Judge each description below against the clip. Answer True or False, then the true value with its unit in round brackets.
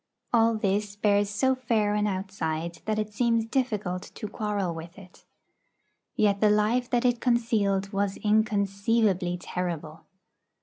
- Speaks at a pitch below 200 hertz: False (210 Hz)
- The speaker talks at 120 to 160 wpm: True (135 wpm)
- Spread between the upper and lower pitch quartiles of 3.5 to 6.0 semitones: False (2.7 semitones)